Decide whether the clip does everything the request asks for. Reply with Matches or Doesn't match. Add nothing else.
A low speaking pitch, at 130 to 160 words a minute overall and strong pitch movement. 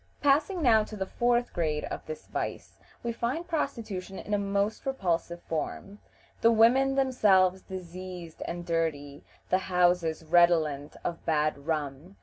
Doesn't match